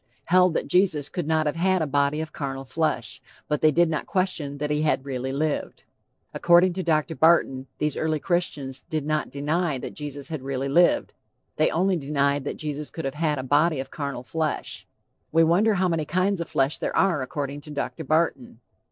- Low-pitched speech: No, medium, 155 Hz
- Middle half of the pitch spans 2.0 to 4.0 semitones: Yes, average, 3.2 semitones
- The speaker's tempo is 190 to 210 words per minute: Yes, average, 200 wpm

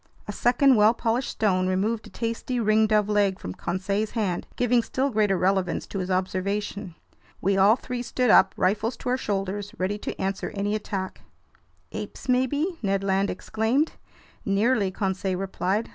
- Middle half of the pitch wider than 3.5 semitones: No, average, 3.2 semitones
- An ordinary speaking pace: Yes, average, 160 wpm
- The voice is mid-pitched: No, high, 205 Hz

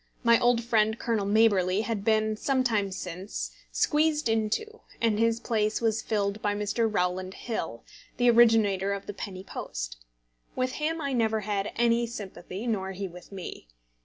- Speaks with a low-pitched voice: No, high, 215 Hz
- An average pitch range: Yes, average, 3.0 semitones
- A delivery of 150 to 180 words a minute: Yes, average, 160 wpm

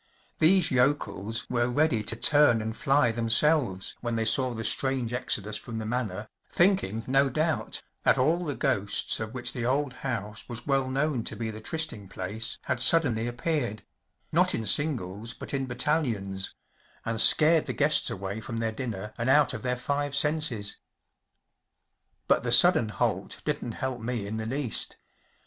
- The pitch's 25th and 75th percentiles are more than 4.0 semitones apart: Yes, average, 4.4 semitones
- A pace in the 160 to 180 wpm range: Yes, average, 165 wpm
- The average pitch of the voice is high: No, low, 120 Hz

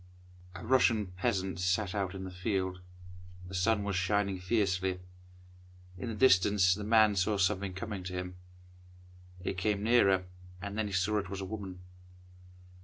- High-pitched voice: No, very low, 95 Hz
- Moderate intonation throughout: No, narrow, 2.3 semitones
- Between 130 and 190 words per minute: Yes, average, 160 wpm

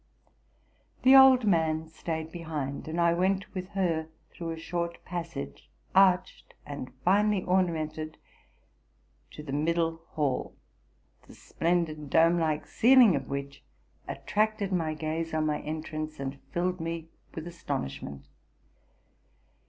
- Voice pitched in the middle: Yes, medium, 165 Hz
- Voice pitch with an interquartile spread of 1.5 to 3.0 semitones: Yes, average, 2.7 semitones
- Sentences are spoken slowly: Yes, slow, 125 wpm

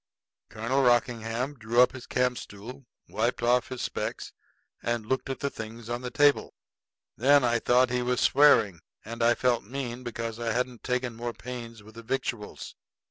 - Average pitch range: No, narrow, 1.6 semitones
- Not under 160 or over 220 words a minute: Yes, average, 170 wpm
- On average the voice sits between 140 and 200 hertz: No, low, 120 Hz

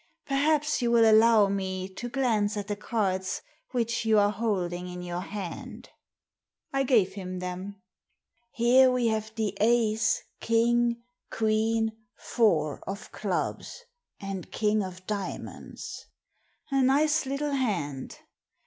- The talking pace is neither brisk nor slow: No, slow, 130 wpm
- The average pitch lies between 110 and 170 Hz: No, high, 215 Hz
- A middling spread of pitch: Yes, average, 3.7 semitones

